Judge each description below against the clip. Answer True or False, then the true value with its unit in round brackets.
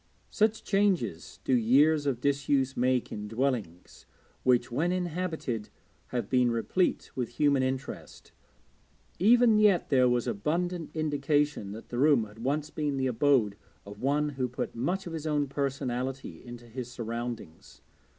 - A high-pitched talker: False (135 Hz)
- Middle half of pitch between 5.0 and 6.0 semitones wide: False (4.0 semitones)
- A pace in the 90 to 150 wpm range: True (145 wpm)